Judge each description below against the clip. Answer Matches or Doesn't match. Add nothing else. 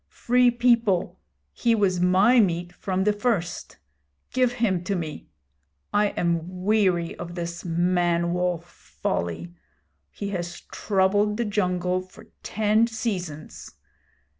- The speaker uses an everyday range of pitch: Matches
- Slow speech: Matches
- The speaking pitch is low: Doesn't match